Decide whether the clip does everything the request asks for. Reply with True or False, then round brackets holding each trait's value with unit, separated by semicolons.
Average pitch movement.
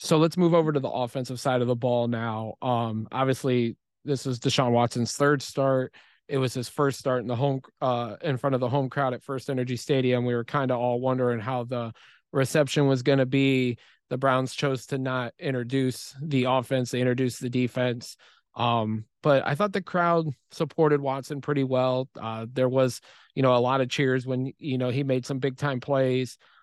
False (2.1 semitones)